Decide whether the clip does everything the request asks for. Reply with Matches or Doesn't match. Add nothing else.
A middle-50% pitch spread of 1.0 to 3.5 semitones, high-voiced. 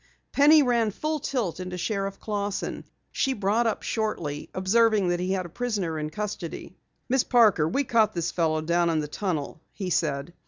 Doesn't match